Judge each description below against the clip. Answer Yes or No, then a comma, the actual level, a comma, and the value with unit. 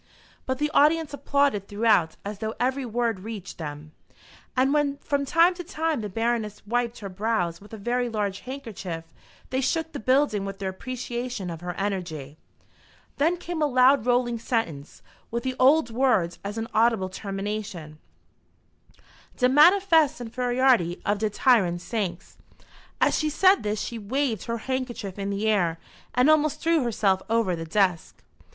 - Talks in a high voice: Yes, high, 230 Hz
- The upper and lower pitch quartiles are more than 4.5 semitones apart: Yes, average, 5.1 semitones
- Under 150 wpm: No, average, 160 wpm